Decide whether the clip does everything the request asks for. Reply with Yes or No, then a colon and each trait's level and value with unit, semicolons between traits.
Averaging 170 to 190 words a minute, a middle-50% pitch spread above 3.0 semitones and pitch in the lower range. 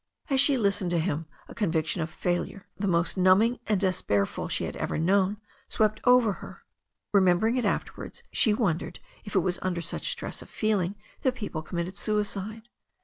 No: average, 175 wpm; average, 3.6 semitones; high, 190 Hz